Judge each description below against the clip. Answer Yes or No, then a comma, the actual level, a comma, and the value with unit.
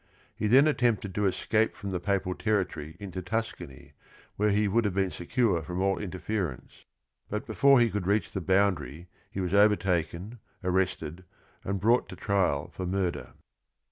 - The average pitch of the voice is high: No, low, 100 Hz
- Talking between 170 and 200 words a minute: No, average, 160 wpm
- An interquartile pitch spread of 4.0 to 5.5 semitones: No, average, 2.8 semitones